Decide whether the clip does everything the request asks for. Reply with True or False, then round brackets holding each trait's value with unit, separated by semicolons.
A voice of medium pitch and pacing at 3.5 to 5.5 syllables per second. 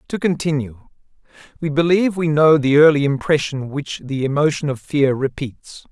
True (145 Hz; 5.0 syllables/s)